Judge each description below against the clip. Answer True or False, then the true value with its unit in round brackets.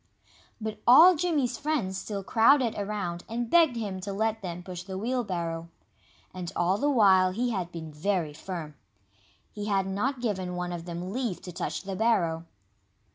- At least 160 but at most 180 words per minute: True (170 wpm)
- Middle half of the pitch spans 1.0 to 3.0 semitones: False (4.6 semitones)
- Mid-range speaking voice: False (195 Hz)